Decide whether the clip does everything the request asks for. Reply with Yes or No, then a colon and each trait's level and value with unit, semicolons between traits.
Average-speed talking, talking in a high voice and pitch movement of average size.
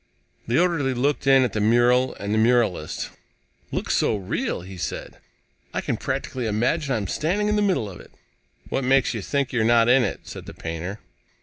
No: average, 195 wpm; low, 120 Hz; average, 4.3 semitones